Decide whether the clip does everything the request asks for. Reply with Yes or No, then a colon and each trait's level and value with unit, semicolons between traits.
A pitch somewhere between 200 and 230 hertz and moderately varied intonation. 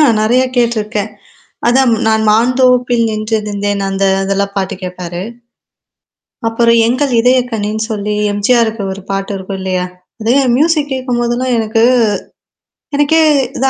Yes: high, 220 Hz; average, 3.4 semitones